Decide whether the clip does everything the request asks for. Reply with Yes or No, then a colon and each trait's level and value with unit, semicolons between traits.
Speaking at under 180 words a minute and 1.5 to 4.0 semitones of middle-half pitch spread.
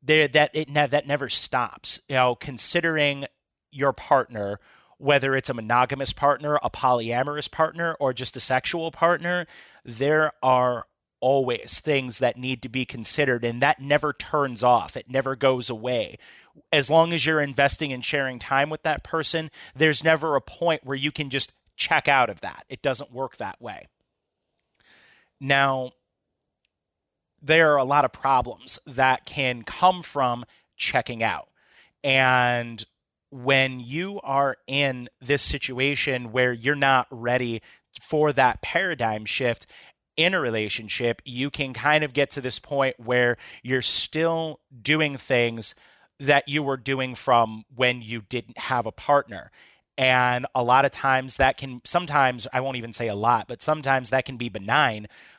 Yes: average, 160 wpm; average, 2.9 semitones